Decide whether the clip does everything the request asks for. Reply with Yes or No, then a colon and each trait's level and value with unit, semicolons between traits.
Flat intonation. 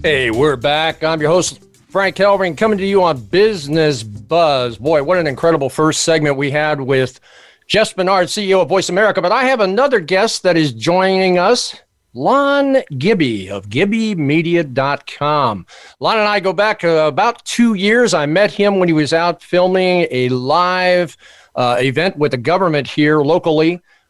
No: average, 4.7 semitones